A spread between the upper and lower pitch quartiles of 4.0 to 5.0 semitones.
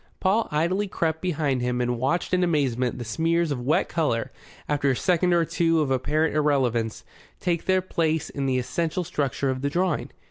Yes: average, 4.7 semitones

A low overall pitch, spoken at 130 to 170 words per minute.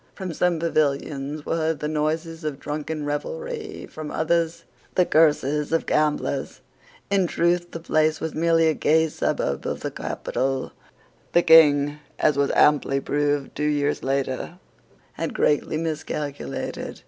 No: medium, 155 Hz; average, 140 wpm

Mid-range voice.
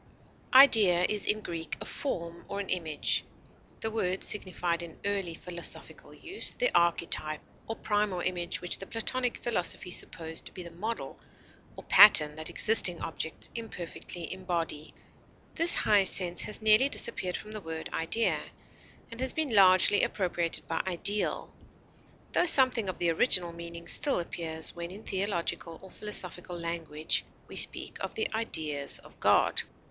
Yes: medium, 180 Hz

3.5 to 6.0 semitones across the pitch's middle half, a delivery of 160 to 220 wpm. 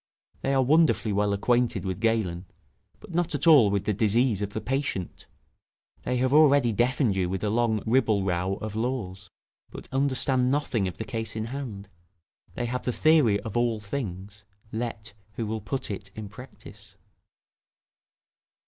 Yes: average, 4.2 semitones; average, 165 wpm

